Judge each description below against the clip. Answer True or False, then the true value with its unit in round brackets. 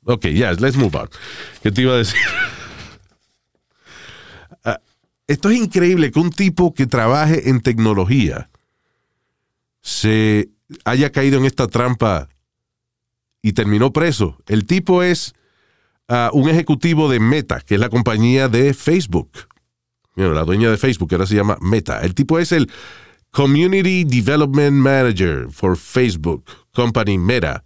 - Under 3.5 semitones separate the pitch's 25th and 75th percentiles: False (5.3 semitones)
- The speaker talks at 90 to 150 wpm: True (140 wpm)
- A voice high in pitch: False (125 Hz)